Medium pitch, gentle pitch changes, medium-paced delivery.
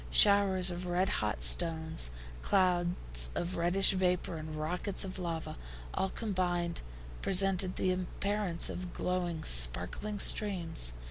No: medium, 180 Hz; narrow, 2.3 semitones; slow, 120 wpm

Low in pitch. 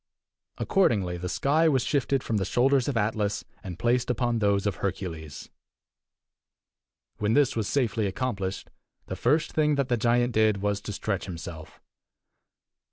Yes: low, 110 Hz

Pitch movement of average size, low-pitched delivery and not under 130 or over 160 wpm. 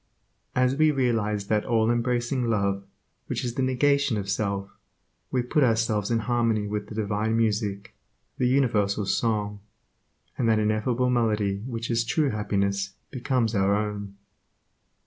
Yes: average, 3.0 semitones; low, 110 Hz; average, 145 wpm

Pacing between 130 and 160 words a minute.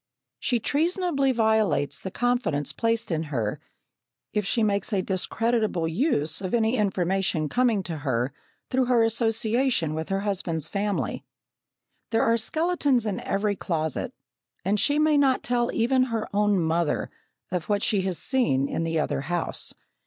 Yes: average, 150 wpm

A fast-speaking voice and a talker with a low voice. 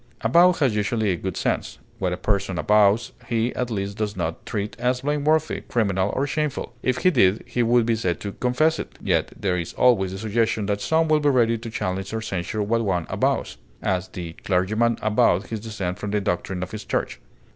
Yes: fast, 210 wpm; low, 110 Hz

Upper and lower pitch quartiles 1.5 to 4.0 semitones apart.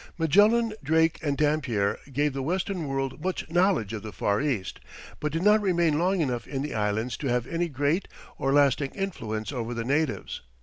No: wide, 5.6 semitones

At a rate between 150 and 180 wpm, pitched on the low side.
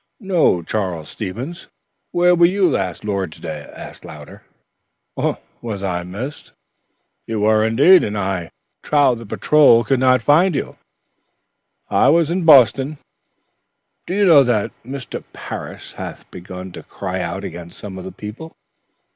No: average, 140 wpm; low, 115 Hz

